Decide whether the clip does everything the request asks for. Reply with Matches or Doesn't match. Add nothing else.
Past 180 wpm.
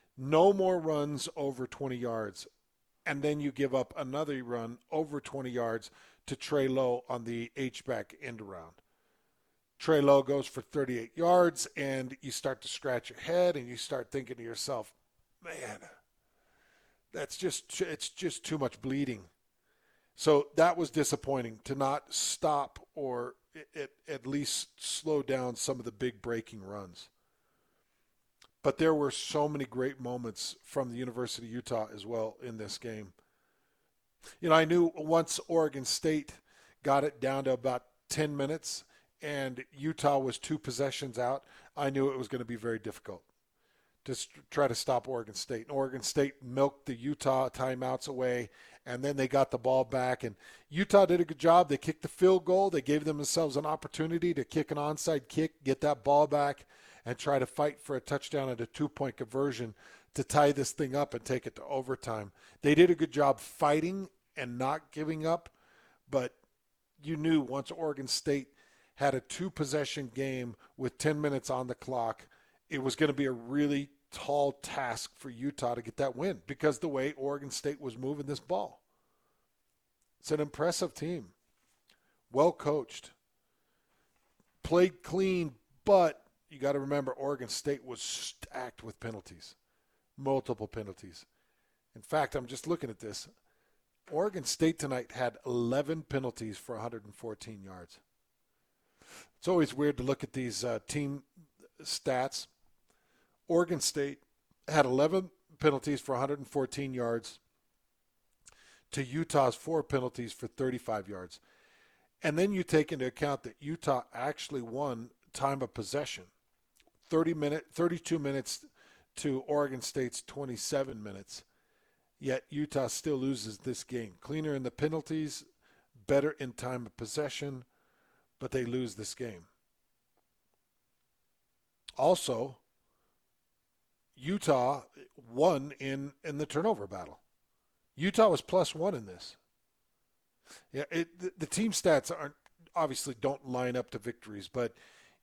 Doesn't match